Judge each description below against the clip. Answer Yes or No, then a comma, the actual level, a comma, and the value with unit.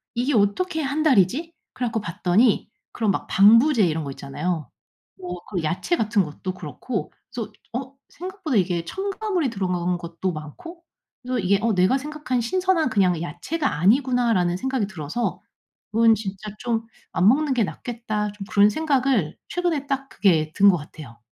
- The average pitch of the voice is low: No, high, 215 Hz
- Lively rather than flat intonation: Yes, wide, 6.9 semitones